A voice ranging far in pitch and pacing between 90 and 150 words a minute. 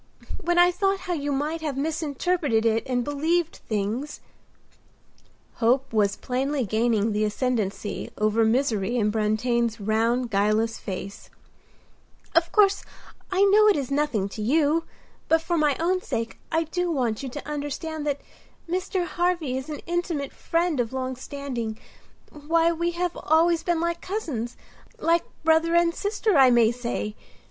Yes: wide, 6.6 semitones; average, 145 wpm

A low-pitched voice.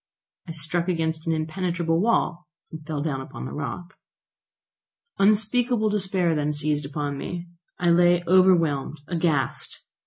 No: medium, 170 Hz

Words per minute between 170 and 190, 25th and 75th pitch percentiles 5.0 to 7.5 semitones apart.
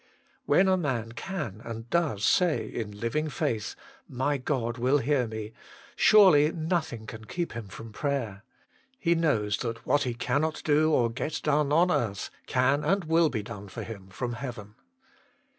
Yes: average, 175 wpm; wide, 5.5 semitones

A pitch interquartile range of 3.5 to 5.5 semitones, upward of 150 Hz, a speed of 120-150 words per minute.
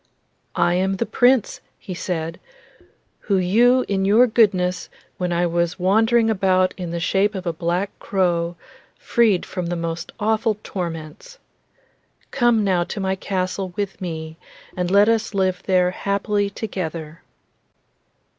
No: average, 3.0 semitones; high, 190 Hz; average, 140 wpm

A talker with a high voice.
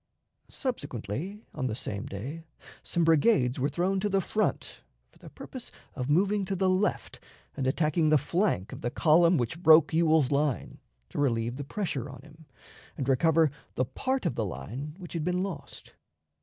No: medium, 155 Hz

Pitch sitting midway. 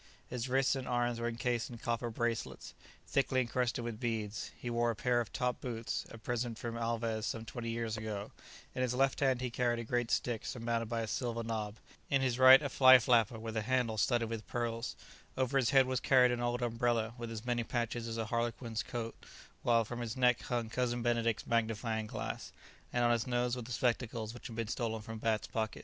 No: low, 120 Hz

